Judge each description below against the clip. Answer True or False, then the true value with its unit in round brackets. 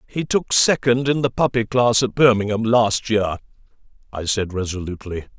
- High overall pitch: False (115 Hz)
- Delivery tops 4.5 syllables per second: True (5.2 syllables/s)